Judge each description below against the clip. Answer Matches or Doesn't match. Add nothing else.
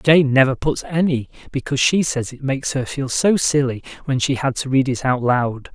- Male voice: Matches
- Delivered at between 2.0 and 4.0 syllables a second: Doesn't match